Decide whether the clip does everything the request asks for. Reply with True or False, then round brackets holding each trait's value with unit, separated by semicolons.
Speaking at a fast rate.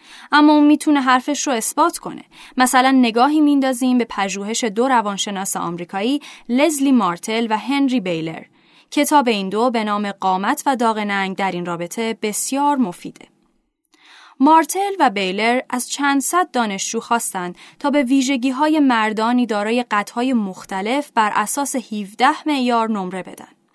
False (135 wpm)